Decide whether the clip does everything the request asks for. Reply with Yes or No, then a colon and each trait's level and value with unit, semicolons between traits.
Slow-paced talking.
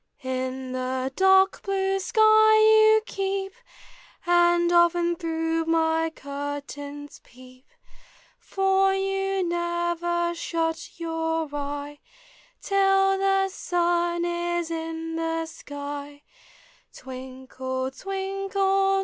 Yes: slow, 80 wpm